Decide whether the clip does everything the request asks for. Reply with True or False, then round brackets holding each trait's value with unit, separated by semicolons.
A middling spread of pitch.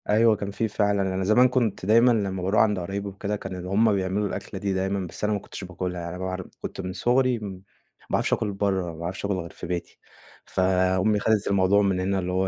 False (2.0 semitones)